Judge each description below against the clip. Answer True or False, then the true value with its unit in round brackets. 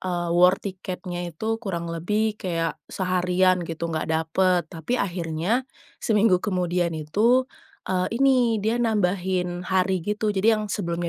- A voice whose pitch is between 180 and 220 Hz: True (185 Hz)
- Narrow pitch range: False (3.3 semitones)